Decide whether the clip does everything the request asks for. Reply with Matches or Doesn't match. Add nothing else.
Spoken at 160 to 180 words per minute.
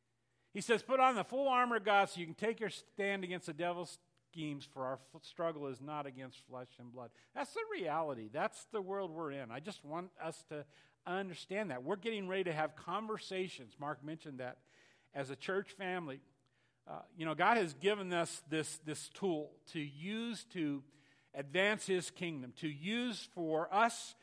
Doesn't match